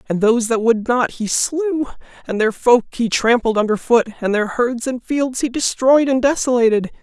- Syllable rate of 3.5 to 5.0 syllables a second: Yes, 4.9 syllables/s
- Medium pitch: No, high, 235 Hz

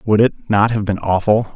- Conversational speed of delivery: No, fast, 230 wpm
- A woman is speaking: No, male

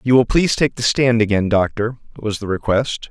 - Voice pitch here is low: Yes, low, 110 Hz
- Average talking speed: No, fast, 215 wpm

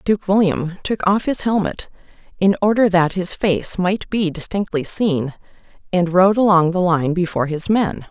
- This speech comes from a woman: Yes, female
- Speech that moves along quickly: No, average, 170 wpm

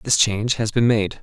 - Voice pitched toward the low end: Yes, low, 110 Hz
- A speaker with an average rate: No, fast, 245 wpm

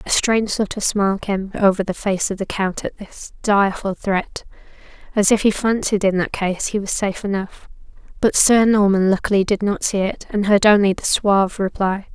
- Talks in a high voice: Yes, high, 200 Hz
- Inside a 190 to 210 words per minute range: Yes, fast, 205 wpm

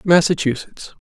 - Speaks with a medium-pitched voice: Yes, medium, 165 Hz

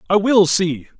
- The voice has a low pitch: No, medium, 185 Hz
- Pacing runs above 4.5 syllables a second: No, 4.3 syllables/s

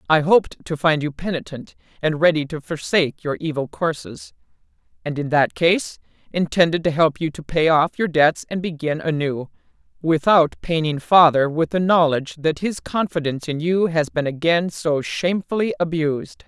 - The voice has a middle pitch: Yes, medium, 160 Hz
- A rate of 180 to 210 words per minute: No, average, 170 wpm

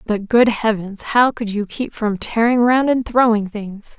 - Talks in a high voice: Yes, high, 225 Hz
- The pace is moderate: Yes, average, 195 wpm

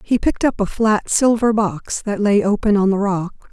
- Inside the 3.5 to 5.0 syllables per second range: Yes, 4.9 syllables/s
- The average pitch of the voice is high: Yes, high, 210 Hz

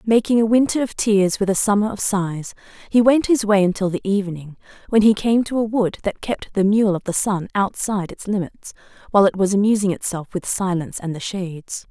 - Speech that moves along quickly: Yes, fast, 215 wpm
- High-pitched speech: Yes, high, 200 Hz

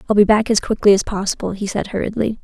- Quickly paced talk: Yes, fast, 245 wpm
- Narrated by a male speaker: No, female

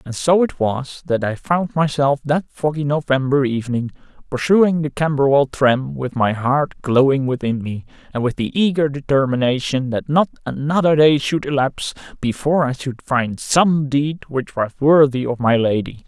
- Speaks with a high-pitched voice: No, medium, 140 Hz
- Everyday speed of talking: Yes, average, 170 wpm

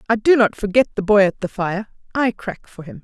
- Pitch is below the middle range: No, high, 205 Hz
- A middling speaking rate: No, fast, 255 wpm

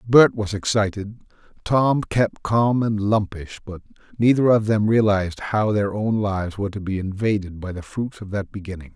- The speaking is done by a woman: No, male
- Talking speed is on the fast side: No, average, 180 wpm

